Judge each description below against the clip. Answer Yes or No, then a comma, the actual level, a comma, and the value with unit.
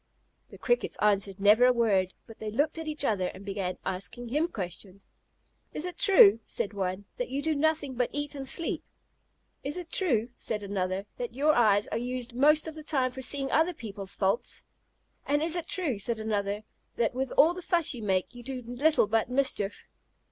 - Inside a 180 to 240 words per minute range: Yes, average, 200 wpm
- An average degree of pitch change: No, wide, 6.4 semitones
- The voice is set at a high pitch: Yes, high, 245 Hz